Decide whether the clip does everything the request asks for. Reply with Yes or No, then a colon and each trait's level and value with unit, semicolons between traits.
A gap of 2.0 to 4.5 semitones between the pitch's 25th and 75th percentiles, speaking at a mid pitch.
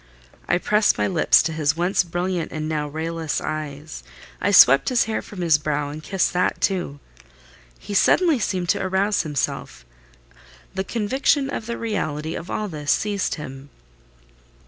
No: average, 5.1 semitones; medium, 170 Hz